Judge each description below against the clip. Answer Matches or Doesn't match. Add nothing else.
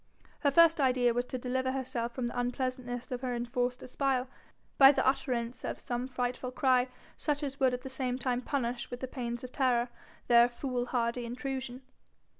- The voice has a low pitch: Doesn't match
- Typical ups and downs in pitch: Doesn't match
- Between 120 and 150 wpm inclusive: Doesn't match